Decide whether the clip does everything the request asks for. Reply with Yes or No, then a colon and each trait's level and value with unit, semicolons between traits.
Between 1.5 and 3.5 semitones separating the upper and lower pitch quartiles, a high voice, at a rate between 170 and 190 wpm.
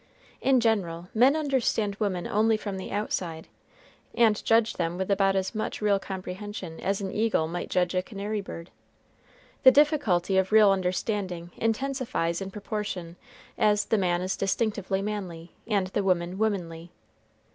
No: average, 3.1 semitones; high, 195 Hz; average, 150 wpm